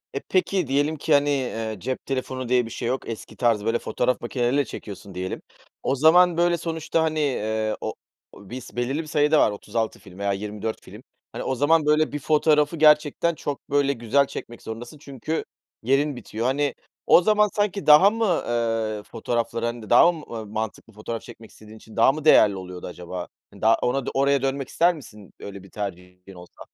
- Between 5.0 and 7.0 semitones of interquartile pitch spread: Yes, wide, 5.5 semitones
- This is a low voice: Yes, low, 125 Hz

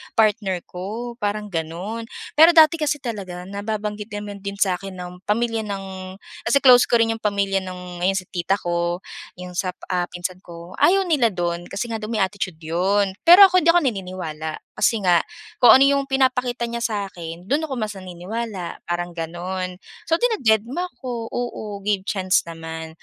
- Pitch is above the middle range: Yes, high, 200 Hz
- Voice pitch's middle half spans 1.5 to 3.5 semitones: No, average, 4.6 semitones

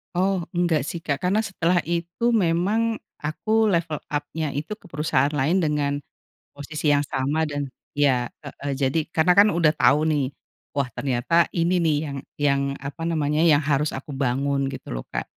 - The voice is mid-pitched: Yes, medium, 150 Hz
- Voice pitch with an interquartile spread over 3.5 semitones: No, average, 3.1 semitones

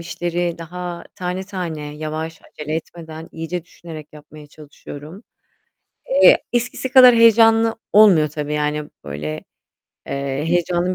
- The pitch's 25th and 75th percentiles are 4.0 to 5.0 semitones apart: No, average, 3.3 semitones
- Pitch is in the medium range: Yes, medium, 165 Hz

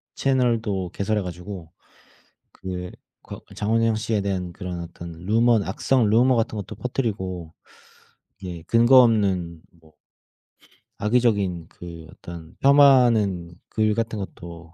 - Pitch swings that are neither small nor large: Yes, average, 4.6 semitones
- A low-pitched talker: Yes, low, 100 Hz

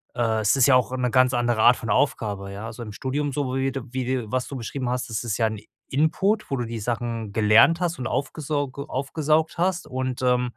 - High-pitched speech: No, low, 125 Hz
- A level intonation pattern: No, average, 3.3 semitones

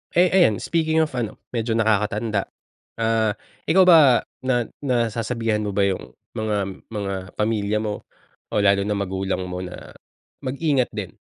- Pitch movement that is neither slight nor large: Yes, average, 3.8 semitones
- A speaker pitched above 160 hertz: No, low, 110 Hz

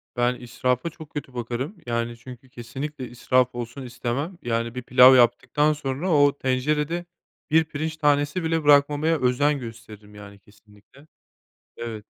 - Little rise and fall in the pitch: No, average, 3.8 semitones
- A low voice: Yes, low, 130 Hz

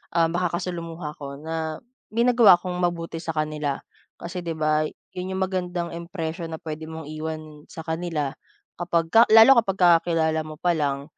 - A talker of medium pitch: Yes, medium, 165 Hz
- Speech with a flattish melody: Yes, narrow, 2.2 semitones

